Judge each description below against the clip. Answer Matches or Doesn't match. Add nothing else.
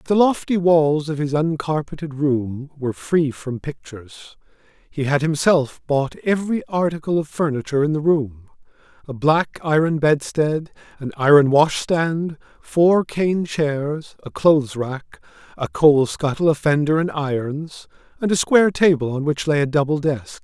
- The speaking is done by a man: Matches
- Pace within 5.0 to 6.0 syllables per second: Doesn't match